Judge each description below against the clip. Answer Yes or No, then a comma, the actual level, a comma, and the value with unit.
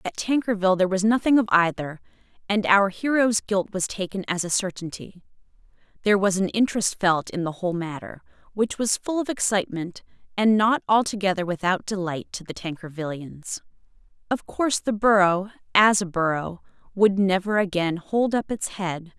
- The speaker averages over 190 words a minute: No, average, 165 wpm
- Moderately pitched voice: No, high, 195 Hz